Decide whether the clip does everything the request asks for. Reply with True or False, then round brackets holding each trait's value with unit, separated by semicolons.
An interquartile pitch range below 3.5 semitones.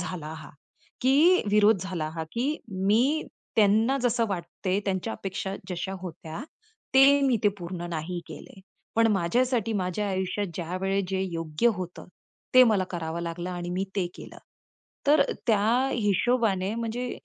False (4.6 semitones)